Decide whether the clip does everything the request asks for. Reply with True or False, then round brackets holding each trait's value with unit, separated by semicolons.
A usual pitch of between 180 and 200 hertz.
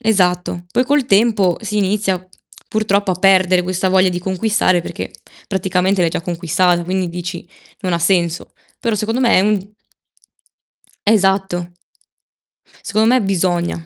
True (190 Hz)